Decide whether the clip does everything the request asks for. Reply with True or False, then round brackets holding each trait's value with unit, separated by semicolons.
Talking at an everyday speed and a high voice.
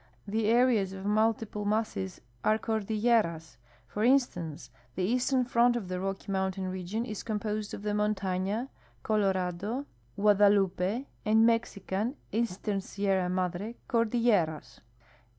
False (120 wpm; 210 Hz)